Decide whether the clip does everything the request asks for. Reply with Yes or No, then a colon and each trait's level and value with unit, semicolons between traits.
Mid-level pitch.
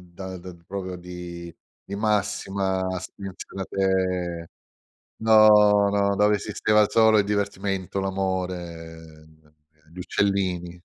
No: very low, 95 Hz